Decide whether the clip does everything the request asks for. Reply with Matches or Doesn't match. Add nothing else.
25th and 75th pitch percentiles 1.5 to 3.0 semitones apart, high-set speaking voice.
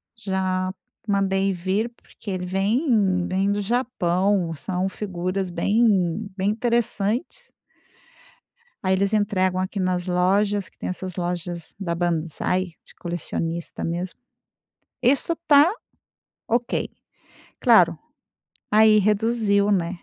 Matches